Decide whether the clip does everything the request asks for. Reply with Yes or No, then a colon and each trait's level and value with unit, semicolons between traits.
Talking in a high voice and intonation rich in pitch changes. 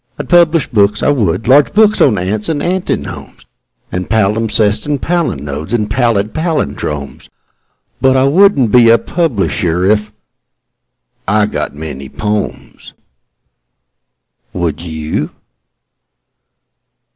No: low, 110 Hz; wide, 7.5 semitones